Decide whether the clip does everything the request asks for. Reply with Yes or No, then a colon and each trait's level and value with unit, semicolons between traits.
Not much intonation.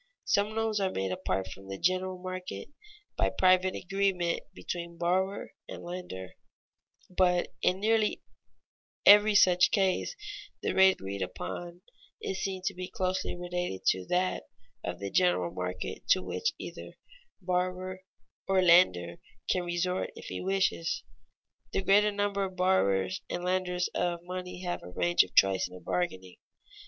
Yes: narrow, 2.0 semitones